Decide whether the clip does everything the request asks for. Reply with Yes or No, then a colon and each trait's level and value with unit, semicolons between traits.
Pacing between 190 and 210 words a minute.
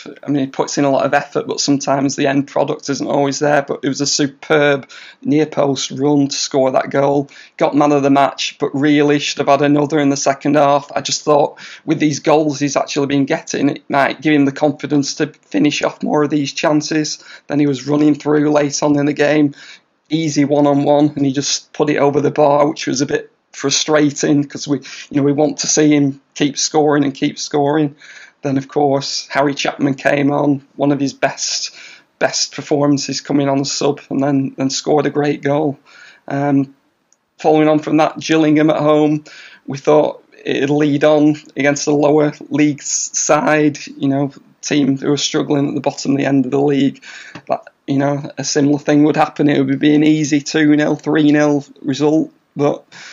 Yes: fast, 205 wpm